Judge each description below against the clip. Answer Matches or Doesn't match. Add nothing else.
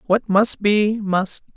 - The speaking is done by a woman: Matches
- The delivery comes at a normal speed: Matches